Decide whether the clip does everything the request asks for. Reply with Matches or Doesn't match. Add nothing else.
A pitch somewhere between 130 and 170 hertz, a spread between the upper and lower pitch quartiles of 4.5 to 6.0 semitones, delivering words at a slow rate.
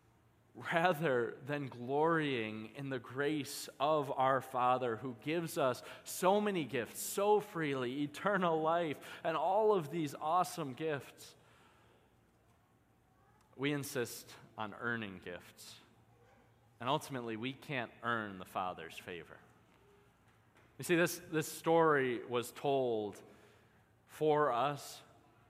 Matches